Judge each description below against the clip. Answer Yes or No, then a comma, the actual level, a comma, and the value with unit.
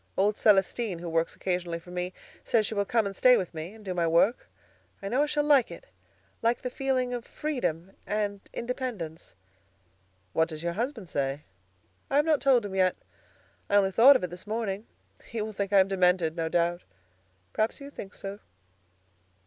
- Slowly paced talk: No, average, 190 wpm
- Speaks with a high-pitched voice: Yes, high, 200 Hz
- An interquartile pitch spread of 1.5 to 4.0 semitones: No, average, 5.2 semitones